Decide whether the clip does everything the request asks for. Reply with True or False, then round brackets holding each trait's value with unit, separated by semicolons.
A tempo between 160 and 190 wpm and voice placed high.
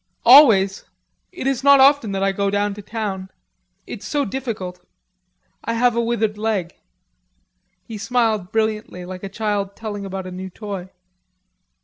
False (150 wpm; 210 Hz)